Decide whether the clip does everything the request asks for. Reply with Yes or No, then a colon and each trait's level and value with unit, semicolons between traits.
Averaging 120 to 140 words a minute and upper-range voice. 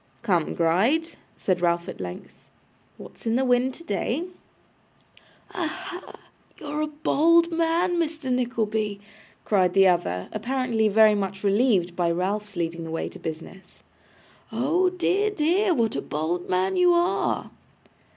Yes: slow, 135 wpm; high, 225 Hz